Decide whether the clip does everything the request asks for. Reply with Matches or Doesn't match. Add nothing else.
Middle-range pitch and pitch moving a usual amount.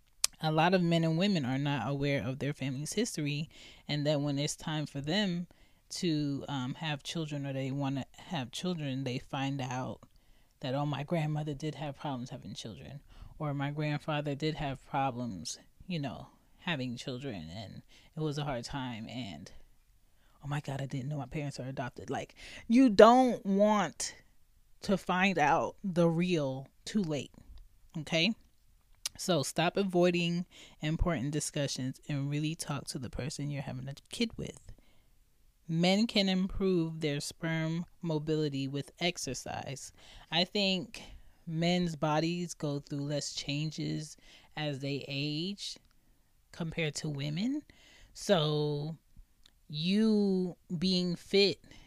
Matches